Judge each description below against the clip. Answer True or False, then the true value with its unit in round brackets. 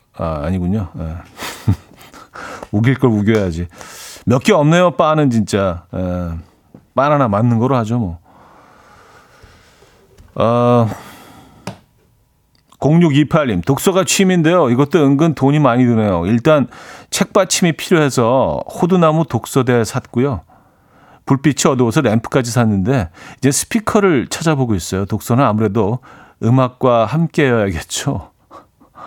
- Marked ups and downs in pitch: True (6.2 semitones)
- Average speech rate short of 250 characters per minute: True (240 characters per minute)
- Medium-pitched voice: False (125 Hz)